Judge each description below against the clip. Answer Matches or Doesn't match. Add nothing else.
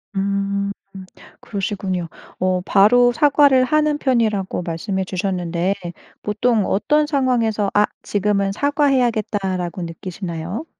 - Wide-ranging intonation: Doesn't match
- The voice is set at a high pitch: Matches